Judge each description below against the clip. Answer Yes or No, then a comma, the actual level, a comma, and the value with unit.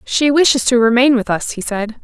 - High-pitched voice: Yes, high, 245 Hz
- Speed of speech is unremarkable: No, fast, 235 wpm